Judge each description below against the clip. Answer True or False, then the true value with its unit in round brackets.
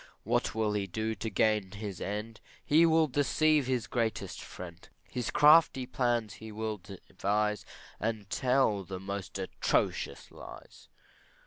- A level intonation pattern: False (3.9 semitones)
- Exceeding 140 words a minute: False (135 wpm)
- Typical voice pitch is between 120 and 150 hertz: False (110 Hz)